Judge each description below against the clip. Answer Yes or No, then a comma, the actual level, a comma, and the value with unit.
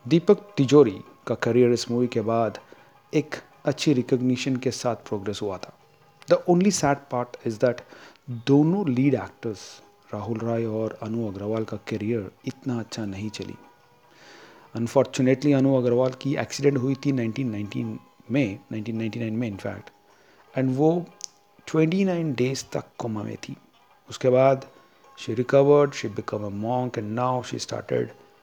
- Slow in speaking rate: No, average, 140 wpm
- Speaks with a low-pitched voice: Yes, low, 125 Hz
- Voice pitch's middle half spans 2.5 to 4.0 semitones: Yes, average, 3.6 semitones